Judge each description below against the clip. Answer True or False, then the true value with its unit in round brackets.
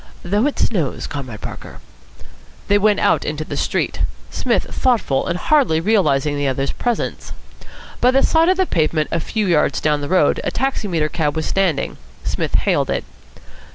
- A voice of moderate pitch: True (170 Hz)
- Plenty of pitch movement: True (6.6 semitones)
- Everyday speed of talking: True (170 wpm)